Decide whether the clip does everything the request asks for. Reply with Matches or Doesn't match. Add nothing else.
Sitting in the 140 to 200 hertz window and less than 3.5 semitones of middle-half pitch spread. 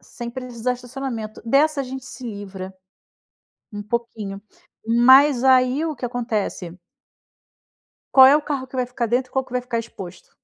Doesn't match